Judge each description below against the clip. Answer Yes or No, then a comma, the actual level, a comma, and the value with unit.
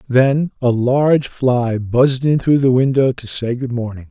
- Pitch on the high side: No, low, 125 Hz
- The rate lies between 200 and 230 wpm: No, average, 190 wpm